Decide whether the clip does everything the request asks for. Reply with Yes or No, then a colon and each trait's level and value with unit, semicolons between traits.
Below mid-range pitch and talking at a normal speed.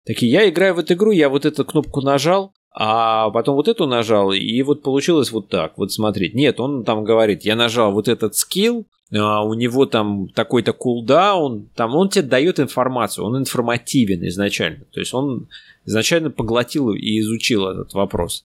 No: low, 120 Hz; fast, 175 wpm